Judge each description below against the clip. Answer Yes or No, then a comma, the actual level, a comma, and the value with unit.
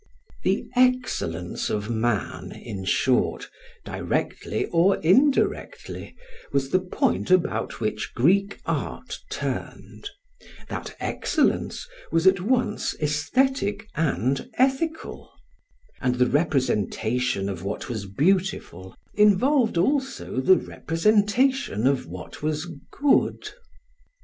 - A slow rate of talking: Yes, slow, 100 wpm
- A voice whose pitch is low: No, medium, 165 Hz